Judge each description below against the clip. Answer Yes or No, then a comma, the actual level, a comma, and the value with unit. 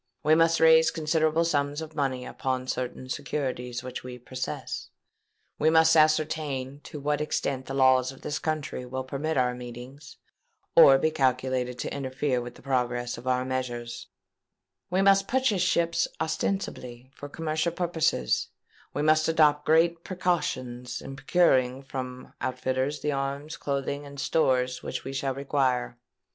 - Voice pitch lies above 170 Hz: No, medium, 140 Hz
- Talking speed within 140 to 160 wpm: Yes, average, 150 wpm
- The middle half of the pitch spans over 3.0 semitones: Yes, average, 3.5 semitones